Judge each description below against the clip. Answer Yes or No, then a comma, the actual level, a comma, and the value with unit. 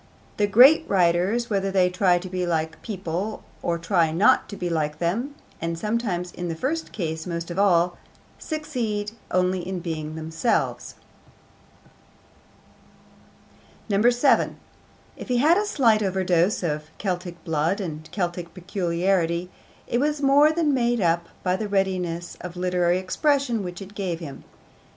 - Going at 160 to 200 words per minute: No, average, 145 wpm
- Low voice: No, medium, 185 Hz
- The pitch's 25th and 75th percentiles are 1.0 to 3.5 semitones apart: No, average, 4.0 semitones